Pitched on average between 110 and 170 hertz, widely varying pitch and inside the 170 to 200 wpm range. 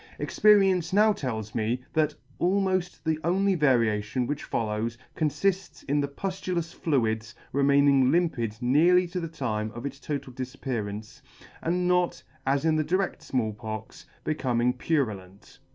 No: medium, 140 Hz; wide, 6.8 semitones; slow, 135 wpm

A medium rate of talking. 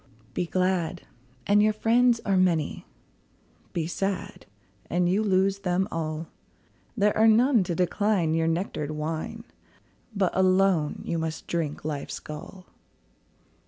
No: slow, 125 wpm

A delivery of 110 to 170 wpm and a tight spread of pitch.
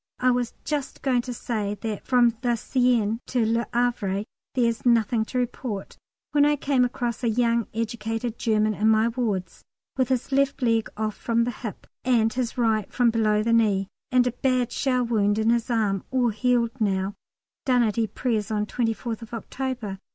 No: average, 180 wpm; narrow, 2.3 semitones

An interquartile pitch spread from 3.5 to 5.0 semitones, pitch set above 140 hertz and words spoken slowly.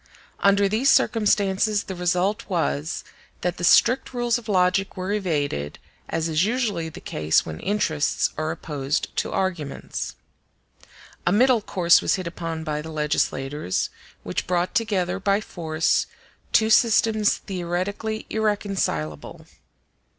Yes: average, 4.7 semitones; medium, 185 Hz; slow, 130 wpm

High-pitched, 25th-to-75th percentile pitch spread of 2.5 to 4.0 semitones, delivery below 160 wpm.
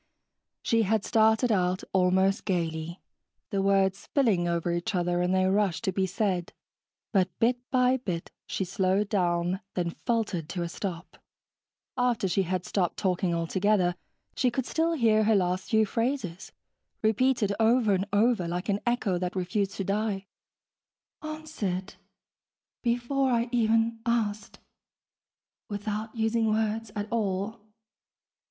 Yes: high, 200 Hz; average, 3.7 semitones; slow, 135 wpm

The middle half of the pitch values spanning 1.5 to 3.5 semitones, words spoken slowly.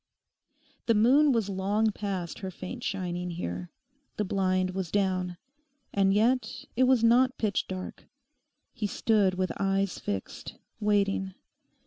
Yes: average, 2.9 semitones; slow, 130 wpm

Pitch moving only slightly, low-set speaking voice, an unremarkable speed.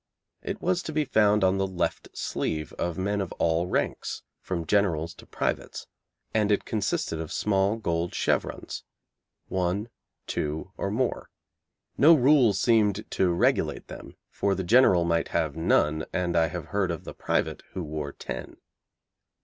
No: average, 4.0 semitones; very low, 95 Hz; average, 155 wpm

